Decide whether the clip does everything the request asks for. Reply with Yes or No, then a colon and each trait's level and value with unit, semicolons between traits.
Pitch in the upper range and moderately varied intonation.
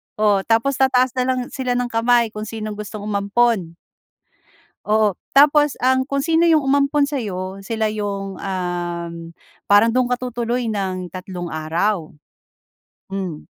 Yes: high, 215 Hz; average, 4.6 semitones